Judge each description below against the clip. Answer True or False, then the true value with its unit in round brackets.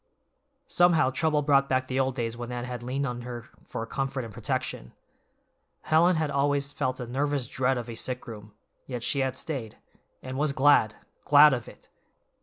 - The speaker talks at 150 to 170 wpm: False (180 wpm)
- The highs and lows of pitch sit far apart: False (2.8 semitones)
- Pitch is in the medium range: False (130 Hz)